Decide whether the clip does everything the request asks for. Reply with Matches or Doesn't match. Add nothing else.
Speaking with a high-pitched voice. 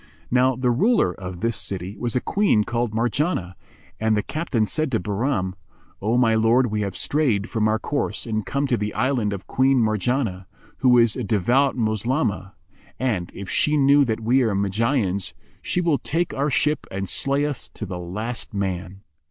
Doesn't match